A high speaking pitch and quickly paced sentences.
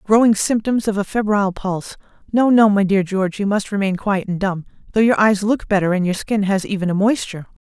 Yes: high, 200 Hz; fast, 220 wpm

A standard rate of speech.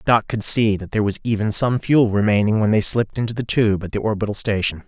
No: fast, 245 wpm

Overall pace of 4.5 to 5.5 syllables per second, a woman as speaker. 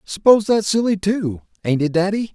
No: 5.0 syllables/s; male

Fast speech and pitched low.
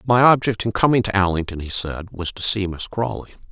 Yes: fast, 220 wpm; low, 105 Hz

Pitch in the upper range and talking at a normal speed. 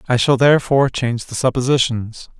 No: low, 130 Hz; average, 150 wpm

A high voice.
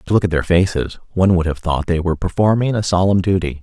No: very low, 90 Hz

